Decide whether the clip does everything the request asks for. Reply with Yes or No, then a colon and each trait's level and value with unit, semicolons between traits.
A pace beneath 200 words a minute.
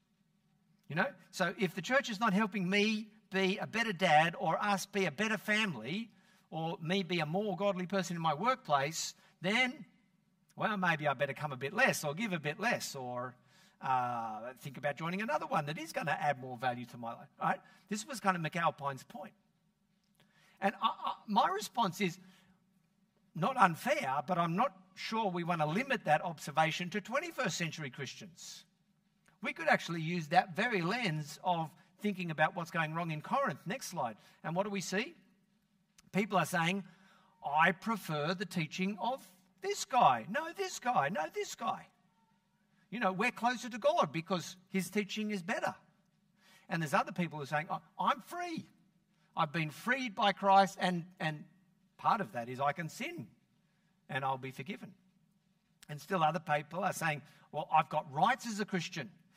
Yes: average, 185 wpm